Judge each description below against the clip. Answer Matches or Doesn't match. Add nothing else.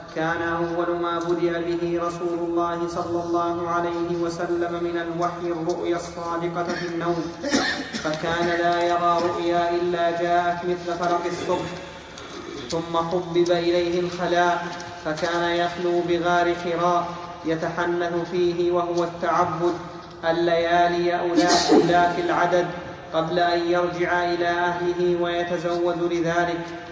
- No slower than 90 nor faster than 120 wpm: Matches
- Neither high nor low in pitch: Matches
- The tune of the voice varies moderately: Doesn't match